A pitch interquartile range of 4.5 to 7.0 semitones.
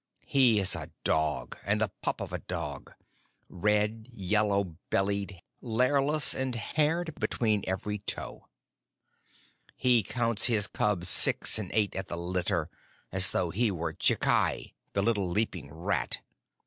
No: average, 4.1 semitones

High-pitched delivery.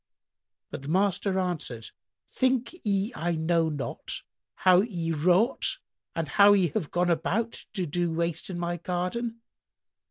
No: medium, 180 Hz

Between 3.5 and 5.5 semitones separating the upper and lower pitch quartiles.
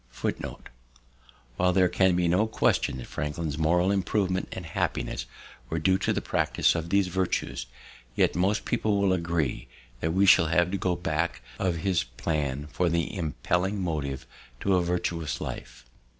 No: average, 3.0 semitones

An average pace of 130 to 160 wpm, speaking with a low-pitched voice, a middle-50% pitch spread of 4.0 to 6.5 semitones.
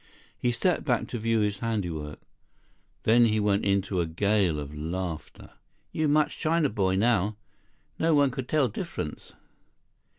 Yes: average, 145 wpm; low, 105 Hz; average, 4.8 semitones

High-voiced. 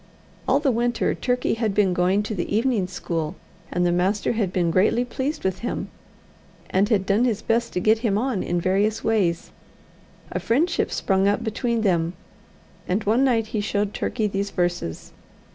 Yes: high, 205 Hz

